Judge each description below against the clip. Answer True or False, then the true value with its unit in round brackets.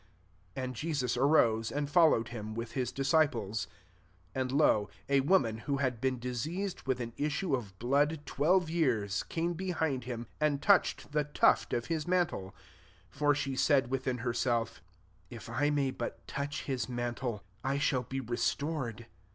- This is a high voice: False (130 Hz)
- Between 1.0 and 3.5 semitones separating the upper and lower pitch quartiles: False (3.9 semitones)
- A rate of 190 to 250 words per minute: False (175 wpm)